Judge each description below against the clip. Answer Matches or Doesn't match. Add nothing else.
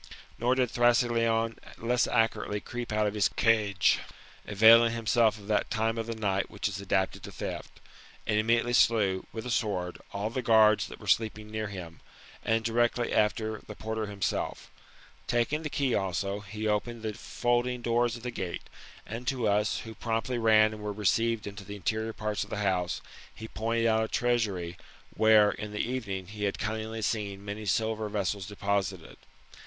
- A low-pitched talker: Matches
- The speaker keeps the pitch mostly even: Matches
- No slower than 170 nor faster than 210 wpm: Matches